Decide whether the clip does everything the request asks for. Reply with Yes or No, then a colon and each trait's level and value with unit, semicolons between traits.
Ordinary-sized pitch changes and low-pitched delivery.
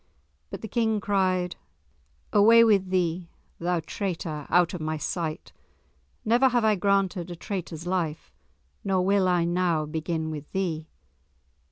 No: average, 3.2 semitones; medium, 180 Hz